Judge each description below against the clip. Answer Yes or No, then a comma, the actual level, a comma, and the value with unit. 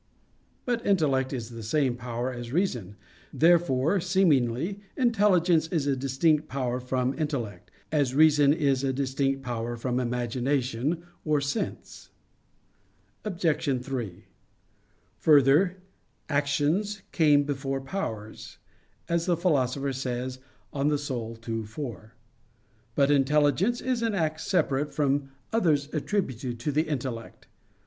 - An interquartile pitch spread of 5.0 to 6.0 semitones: No, average, 4.2 semitones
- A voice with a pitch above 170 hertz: No, medium, 140 Hz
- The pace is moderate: No, slow, 115 wpm